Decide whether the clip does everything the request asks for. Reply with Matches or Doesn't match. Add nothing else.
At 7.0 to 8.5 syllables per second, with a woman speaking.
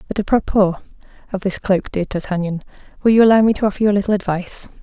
Matches